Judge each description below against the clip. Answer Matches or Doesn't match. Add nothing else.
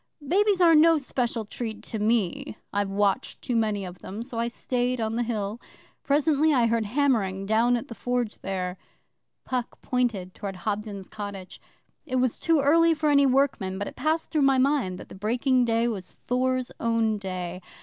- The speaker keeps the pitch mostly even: Doesn't match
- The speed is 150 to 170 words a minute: Doesn't match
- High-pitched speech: Matches